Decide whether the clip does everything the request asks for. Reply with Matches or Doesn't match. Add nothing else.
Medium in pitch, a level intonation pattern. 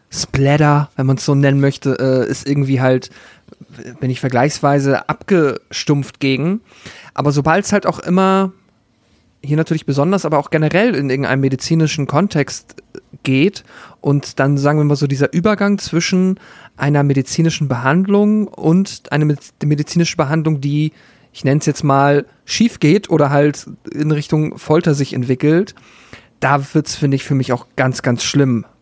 Doesn't match